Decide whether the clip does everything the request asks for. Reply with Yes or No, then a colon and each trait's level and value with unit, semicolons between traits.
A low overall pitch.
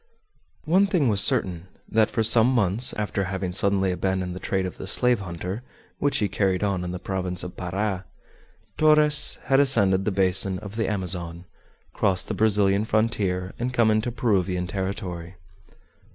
Yes: low, 100 Hz